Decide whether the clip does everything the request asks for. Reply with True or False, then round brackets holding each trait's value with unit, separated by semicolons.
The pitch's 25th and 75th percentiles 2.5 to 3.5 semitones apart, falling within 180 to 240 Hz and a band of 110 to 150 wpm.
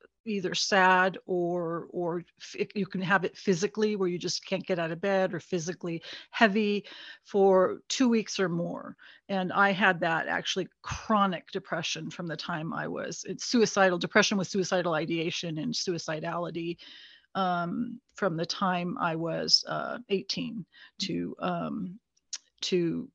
True (2.9 semitones; 185 Hz; 145 wpm)